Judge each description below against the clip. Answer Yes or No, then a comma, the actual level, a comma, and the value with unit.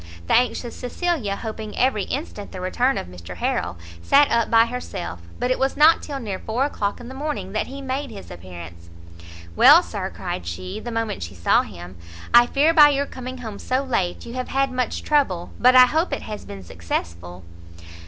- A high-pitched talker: Yes, high, 230 Hz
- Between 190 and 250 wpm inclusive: Yes, average, 200 wpm